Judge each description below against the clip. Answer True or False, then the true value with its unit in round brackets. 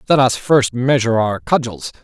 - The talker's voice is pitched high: False (120 Hz)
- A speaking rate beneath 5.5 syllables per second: True (5.1 syllables/s)